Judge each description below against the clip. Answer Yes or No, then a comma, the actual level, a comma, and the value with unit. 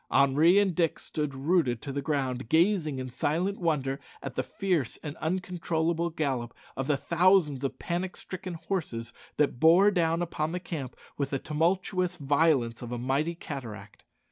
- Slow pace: No, average, 165 wpm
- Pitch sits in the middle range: Yes, medium, 155 Hz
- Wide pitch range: No, average, 4.4 semitones